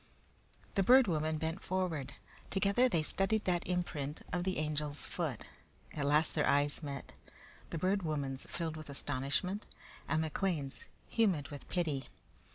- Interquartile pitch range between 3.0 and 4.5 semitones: Yes, average, 4.2 semitones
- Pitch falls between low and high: Yes, medium, 160 Hz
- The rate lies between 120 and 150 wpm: Yes, average, 145 wpm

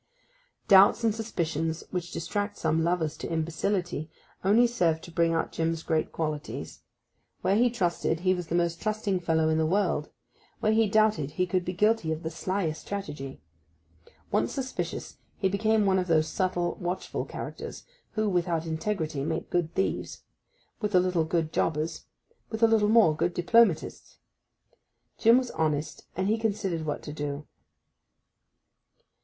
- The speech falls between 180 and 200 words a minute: No, average, 155 wpm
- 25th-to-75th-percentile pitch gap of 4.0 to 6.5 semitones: Yes, average, 4.3 semitones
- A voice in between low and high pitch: Yes, medium, 175 Hz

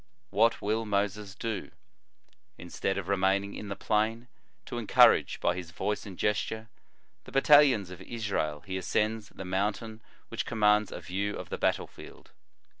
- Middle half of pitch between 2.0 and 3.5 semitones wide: Yes, narrow, 2.5 semitones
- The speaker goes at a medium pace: Yes, average, 155 wpm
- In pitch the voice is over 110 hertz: No, low, 105 Hz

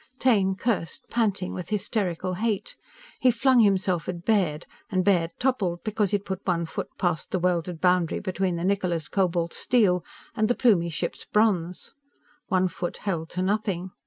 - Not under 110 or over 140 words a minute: No, average, 160 wpm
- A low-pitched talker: No, medium, 185 Hz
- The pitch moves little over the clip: No, average, 3.2 semitones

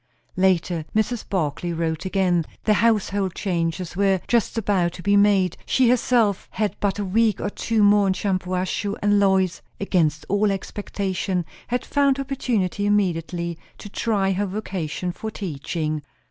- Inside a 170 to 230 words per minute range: No, average, 145 wpm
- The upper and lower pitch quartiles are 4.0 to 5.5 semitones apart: No, average, 2.7 semitones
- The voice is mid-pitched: No, high, 195 Hz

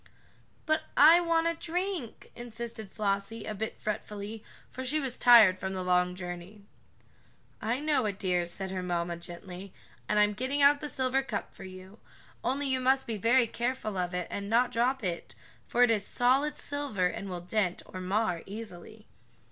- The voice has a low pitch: No, high, 215 Hz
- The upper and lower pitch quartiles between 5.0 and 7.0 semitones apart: Yes, wide, 5.6 semitones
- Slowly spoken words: No, average, 180 wpm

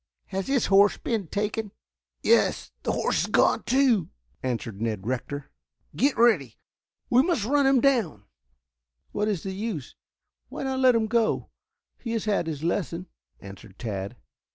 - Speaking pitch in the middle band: No, high, 205 Hz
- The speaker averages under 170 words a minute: Yes, average, 160 wpm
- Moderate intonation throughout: No, wide, 8.6 semitones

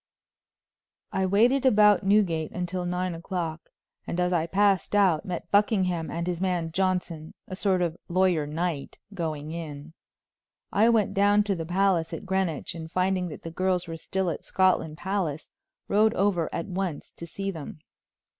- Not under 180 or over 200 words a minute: No, average, 165 wpm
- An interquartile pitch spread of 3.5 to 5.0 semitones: No, average, 2.9 semitones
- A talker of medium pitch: Yes, medium, 180 Hz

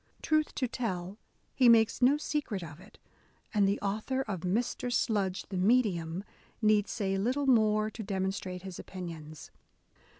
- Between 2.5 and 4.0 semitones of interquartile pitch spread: No, average, 4.4 semitones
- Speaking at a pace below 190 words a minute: Yes, average, 145 wpm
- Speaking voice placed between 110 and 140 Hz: No, high, 205 Hz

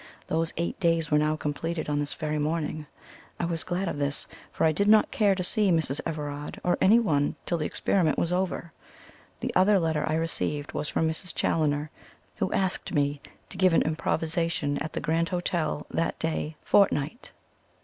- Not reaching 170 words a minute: No, average, 180 wpm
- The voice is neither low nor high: Yes, medium, 160 Hz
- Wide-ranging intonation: No, average, 2.7 semitones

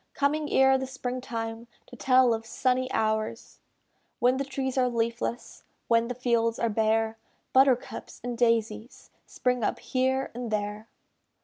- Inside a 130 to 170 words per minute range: Yes, average, 145 wpm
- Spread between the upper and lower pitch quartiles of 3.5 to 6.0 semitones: No, narrow, 2.4 semitones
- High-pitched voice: Yes, high, 240 Hz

